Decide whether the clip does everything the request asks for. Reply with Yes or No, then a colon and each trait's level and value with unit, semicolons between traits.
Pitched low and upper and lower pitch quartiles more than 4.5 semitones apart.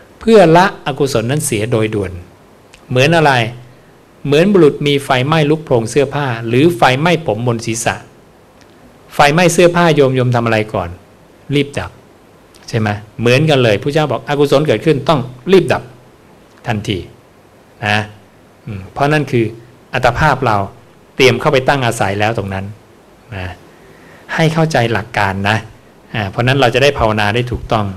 Yes: low, 120 Hz; average, 5.3 semitones